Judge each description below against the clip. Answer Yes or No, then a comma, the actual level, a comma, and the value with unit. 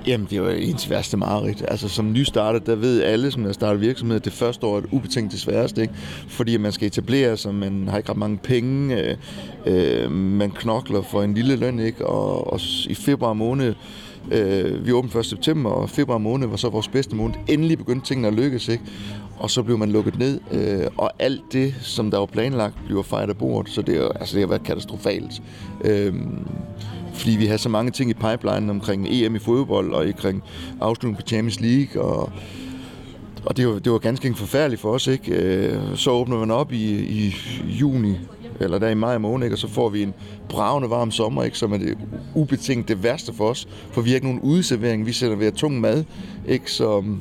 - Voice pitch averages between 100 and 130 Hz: Yes, low, 115 Hz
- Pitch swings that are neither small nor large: Yes, average, 3.1 semitones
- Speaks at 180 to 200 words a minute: No, average, 215 wpm